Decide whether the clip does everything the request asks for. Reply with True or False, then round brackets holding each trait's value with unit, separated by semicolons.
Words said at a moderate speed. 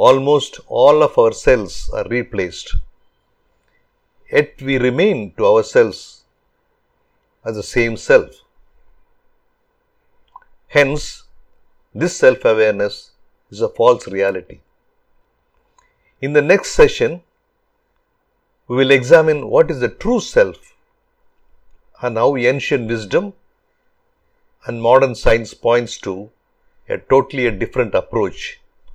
False (100 wpm)